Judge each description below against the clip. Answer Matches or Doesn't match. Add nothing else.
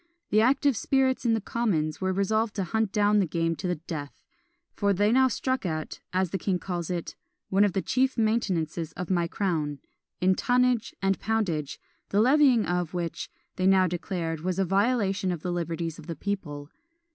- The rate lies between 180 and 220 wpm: Matches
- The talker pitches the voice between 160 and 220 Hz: Matches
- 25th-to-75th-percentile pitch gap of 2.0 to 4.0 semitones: Doesn't match